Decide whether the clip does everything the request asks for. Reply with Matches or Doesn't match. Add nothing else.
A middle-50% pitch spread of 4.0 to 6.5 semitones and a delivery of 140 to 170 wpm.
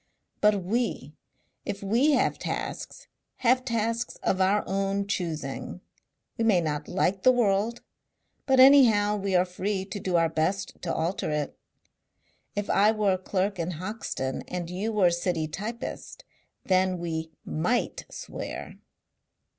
Doesn't match